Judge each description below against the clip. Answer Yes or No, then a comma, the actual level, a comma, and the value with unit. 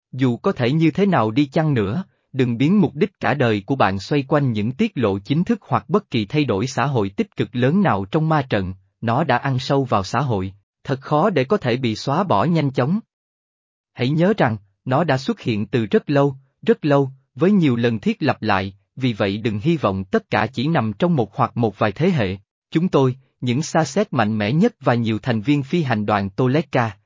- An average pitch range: No, wide, 6.4 semitones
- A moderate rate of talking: Yes, average, 235 wpm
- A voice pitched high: No, low, 130 Hz